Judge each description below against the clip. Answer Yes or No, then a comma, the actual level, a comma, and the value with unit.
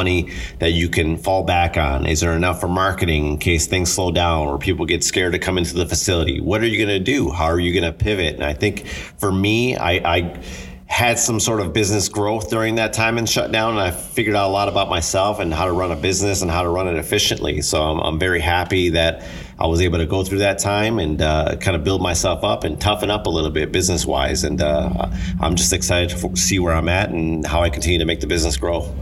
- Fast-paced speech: Yes, fast, 250 wpm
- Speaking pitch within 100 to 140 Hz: No, very low, 90 Hz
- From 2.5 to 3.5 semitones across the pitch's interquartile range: Yes, average, 2.8 semitones